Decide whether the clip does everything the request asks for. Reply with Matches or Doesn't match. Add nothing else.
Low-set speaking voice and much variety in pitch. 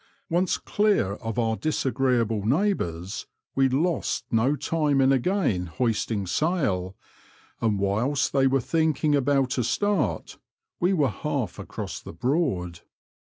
Matches